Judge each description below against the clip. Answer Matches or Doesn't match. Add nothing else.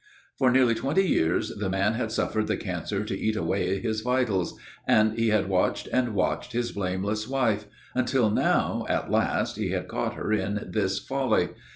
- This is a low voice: Matches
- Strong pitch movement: Doesn't match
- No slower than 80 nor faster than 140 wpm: Doesn't match